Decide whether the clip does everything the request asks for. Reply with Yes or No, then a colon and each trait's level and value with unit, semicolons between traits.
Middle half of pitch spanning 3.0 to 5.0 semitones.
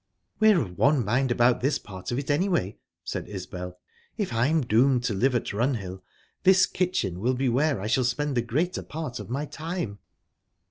No: wide, 5.6 semitones